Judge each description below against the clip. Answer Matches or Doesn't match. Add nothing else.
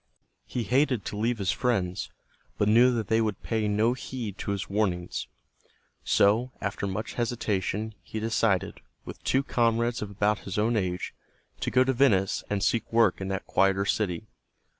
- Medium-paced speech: Matches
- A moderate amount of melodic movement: Matches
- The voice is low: Matches